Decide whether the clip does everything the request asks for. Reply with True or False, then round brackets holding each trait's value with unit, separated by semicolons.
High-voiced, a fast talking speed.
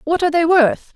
True (325 Hz; 250 wpm)